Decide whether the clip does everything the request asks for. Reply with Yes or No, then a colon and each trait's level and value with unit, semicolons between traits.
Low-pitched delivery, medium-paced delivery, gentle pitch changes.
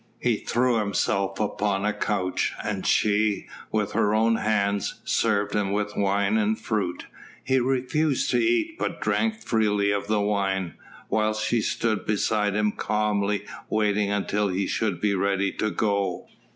Yes: low, 105 Hz; average, 150 wpm; narrow, 1.5 semitones